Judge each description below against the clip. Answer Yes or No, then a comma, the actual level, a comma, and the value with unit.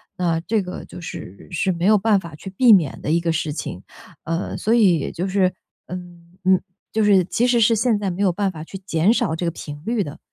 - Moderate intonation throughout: Yes, average, 3.6 semitones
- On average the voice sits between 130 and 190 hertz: Yes, medium, 185 Hz